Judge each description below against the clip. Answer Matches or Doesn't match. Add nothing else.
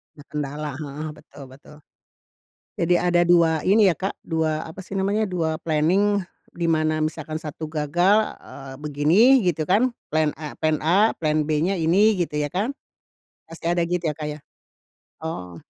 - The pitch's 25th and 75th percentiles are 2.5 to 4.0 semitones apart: Matches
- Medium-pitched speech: Matches